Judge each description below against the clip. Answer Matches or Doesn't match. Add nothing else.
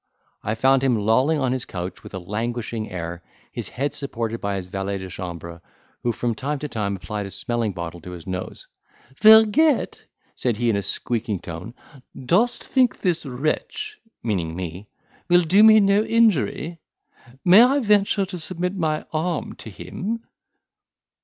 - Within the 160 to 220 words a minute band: Matches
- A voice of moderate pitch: Doesn't match